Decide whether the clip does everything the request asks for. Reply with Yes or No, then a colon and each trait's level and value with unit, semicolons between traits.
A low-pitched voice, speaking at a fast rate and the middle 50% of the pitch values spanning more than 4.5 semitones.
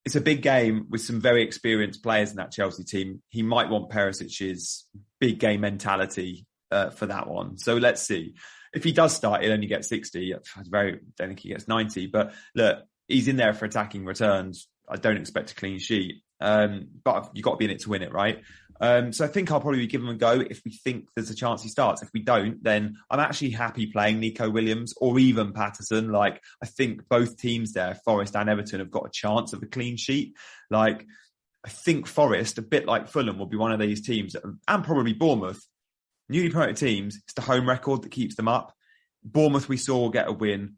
No: low, 110 Hz; fast, 220 wpm; average, 3.6 semitones